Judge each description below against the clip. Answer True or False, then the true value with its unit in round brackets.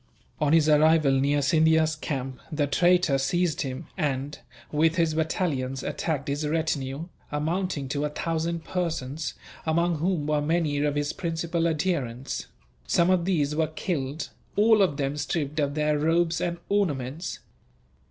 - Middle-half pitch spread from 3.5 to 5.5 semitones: False (2.7 semitones)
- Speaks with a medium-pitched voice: True (155 Hz)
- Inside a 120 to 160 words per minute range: True (150 wpm)